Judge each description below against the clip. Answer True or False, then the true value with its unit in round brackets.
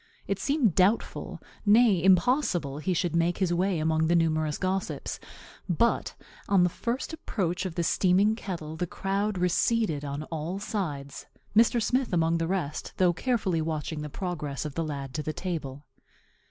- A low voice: False (175 Hz)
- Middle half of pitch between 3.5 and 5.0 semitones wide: True (4.0 semitones)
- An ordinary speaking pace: True (165 wpm)